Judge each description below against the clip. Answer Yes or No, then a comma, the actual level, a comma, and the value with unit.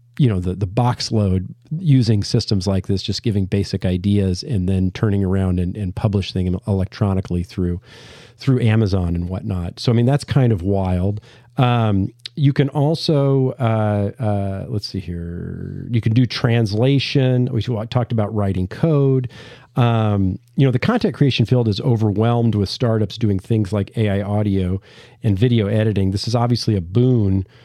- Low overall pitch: Yes, low, 110 Hz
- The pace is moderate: Yes, average, 165 wpm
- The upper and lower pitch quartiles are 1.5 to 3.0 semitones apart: No, average, 4.0 semitones